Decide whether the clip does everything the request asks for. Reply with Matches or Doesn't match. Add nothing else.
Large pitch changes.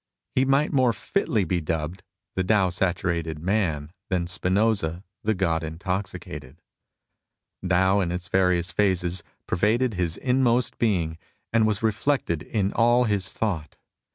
Doesn't match